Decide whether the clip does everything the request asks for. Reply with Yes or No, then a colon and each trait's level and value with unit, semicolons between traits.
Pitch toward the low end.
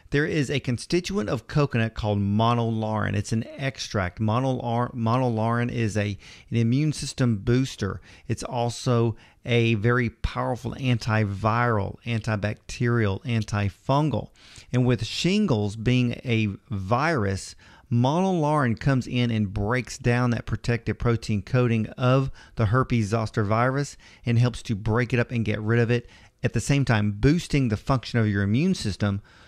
Yes: low, 115 Hz